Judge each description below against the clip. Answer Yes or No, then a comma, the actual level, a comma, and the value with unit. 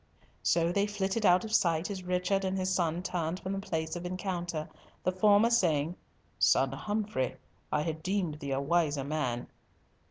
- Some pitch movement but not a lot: Yes, average, 3.5 semitones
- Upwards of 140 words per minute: Yes, average, 170 wpm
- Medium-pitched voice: Yes, medium, 175 Hz